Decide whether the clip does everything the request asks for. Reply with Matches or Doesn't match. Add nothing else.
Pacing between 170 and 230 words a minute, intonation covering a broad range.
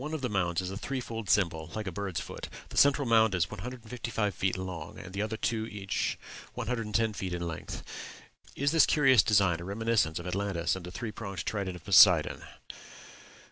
Doesn't match